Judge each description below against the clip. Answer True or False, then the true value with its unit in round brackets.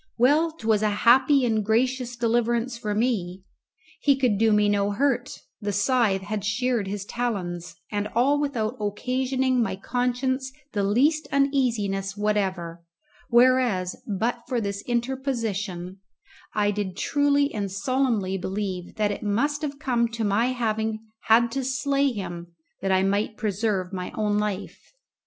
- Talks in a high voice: True (220 Hz)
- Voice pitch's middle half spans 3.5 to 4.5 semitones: True (4.0 semitones)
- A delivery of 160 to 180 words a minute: False (145 wpm)